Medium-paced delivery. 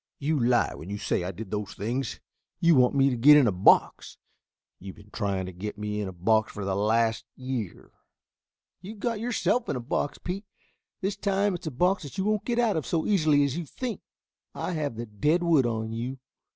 No: fast, 220 wpm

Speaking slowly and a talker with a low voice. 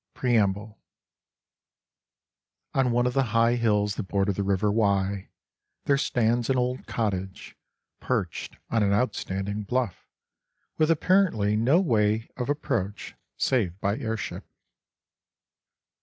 Yes: slow, 120 wpm; low, 110 Hz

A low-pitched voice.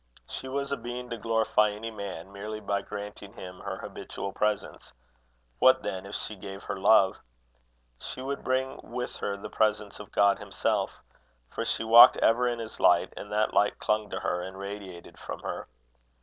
Yes: low, 105 Hz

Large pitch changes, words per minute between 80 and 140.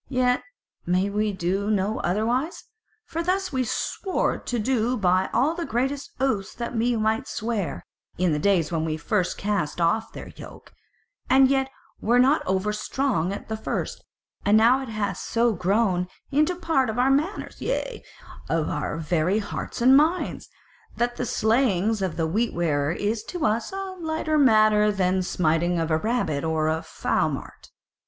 No: wide, 6.1 semitones; average, 175 wpm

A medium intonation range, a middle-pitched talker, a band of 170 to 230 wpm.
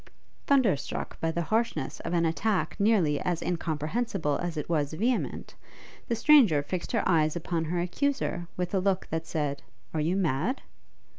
No: average, 4.5 semitones; medium, 175 Hz; average, 160 wpm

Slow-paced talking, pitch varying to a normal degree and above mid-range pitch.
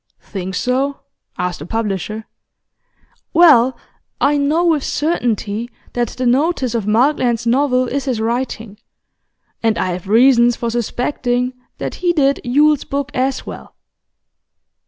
Yes: slow, 130 wpm; average, 3.8 semitones; high, 245 Hz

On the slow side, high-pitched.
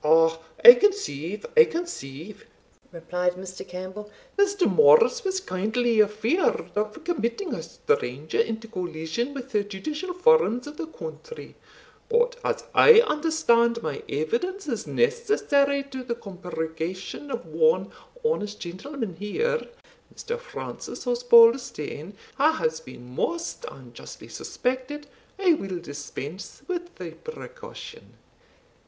Yes: slow, 120 wpm; high, 240 Hz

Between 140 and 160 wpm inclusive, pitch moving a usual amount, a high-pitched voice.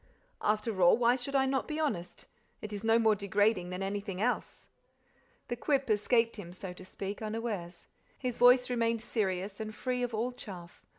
No: average, 180 wpm; average, 3.9 semitones; high, 220 Hz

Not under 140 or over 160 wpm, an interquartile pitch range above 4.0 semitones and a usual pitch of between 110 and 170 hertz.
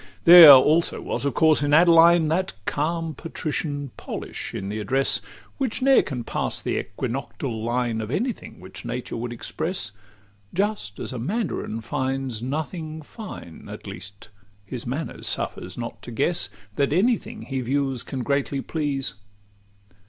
Yes: average, 155 wpm; average, 5.3 semitones; medium, 140 Hz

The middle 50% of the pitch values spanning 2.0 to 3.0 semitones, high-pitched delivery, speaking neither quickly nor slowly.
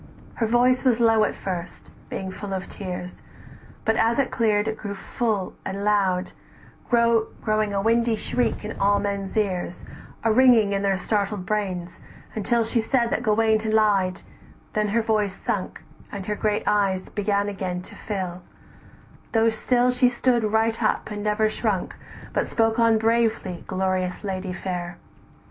Yes: average, 2.7 semitones; high, 210 Hz; average, 160 wpm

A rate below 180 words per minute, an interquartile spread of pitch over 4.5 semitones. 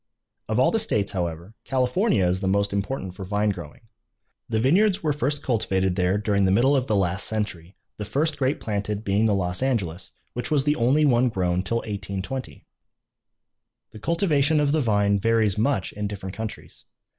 No: average, 185 wpm; wide, 5.5 semitones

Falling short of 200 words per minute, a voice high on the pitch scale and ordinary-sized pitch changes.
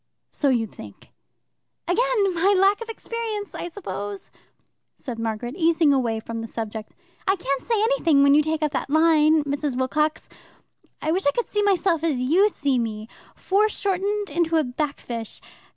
No: average, 165 wpm; very high, 310 Hz; wide, 7.2 semitones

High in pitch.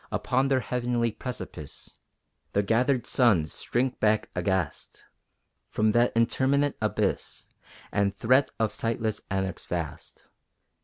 No: low, 115 Hz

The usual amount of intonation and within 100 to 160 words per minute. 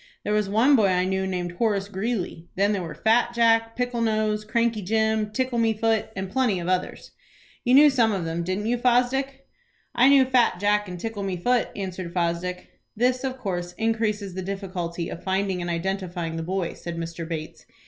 No: average, 4.2 semitones; average, 195 wpm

